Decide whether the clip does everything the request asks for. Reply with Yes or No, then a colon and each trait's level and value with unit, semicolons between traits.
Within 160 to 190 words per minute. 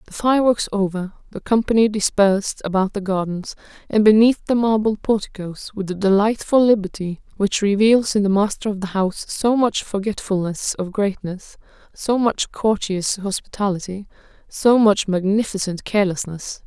No: average, 140 wpm